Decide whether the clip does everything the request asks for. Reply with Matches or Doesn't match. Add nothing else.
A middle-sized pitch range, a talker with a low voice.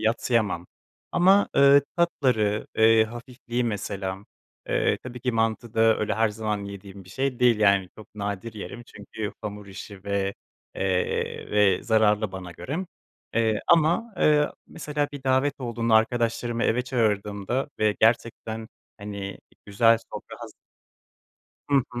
Matches